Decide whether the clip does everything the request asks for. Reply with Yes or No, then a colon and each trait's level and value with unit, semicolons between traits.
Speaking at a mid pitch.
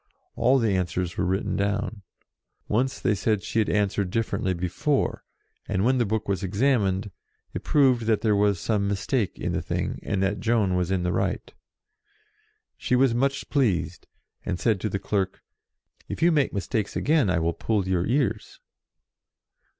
No: low, 105 Hz